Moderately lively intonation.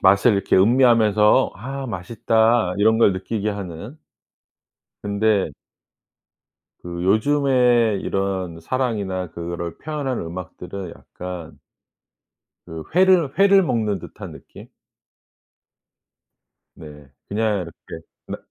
Yes: average, 4.8 semitones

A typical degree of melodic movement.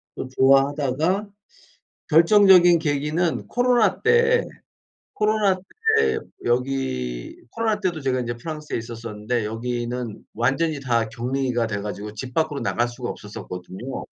No: wide, 7.2 semitones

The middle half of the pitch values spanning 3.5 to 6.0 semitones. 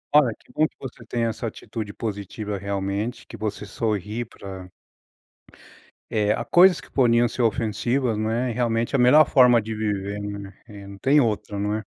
No: average, 2.9 semitones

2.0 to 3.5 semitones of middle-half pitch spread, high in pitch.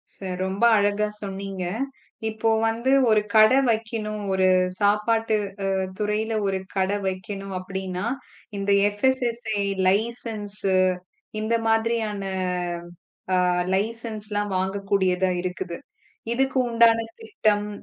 Yes: narrow, 2.4 semitones; high, 210 Hz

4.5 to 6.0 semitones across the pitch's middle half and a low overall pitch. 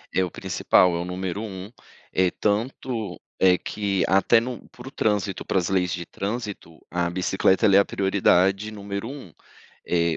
No: average, 2.7 semitones; very low, 95 Hz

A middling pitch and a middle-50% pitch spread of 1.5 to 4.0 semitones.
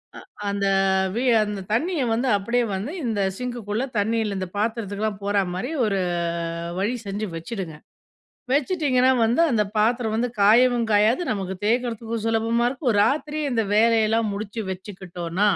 No: high, 220 Hz; average, 3.0 semitones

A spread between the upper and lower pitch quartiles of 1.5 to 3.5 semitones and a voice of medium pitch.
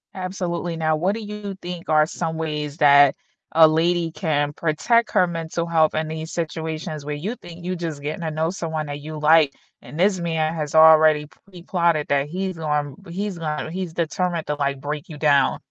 Yes: narrow, 2.4 semitones; medium, 160 Hz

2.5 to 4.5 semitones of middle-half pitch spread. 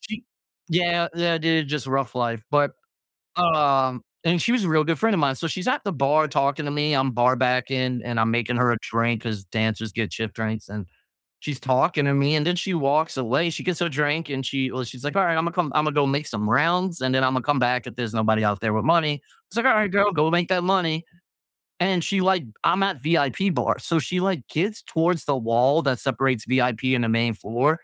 No: average, 5.2 semitones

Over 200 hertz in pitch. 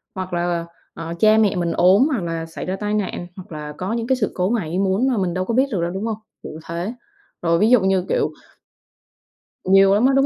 No: high, 190 Hz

